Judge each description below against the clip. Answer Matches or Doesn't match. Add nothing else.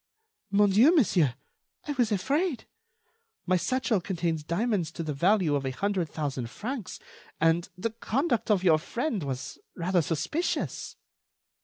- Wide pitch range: Matches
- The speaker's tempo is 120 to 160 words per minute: Matches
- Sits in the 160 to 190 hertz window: Matches